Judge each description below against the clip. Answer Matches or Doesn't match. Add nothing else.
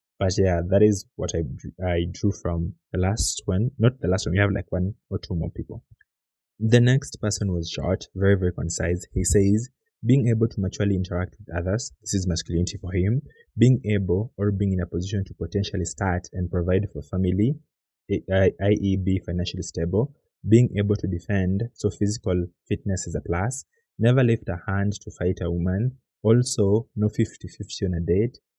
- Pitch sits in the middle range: Doesn't match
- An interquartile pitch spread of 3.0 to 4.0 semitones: Matches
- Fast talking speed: Doesn't match